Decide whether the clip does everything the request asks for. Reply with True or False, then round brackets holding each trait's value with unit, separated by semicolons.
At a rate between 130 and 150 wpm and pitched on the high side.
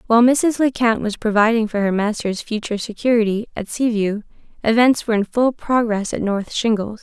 False (180 wpm; 225 Hz)